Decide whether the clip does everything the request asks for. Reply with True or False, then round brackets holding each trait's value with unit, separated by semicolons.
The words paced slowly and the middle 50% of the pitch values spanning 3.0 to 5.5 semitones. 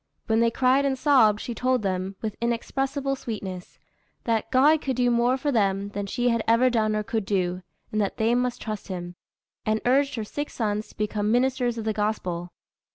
False (200 wpm; 3.4 semitones)